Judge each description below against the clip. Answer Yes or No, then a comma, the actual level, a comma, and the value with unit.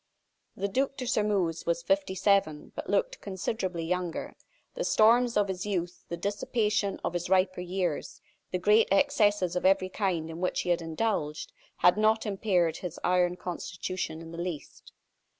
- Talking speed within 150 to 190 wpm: Yes, average, 165 wpm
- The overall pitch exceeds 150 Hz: Yes, medium, 185 Hz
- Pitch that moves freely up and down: No, average, 3.1 semitones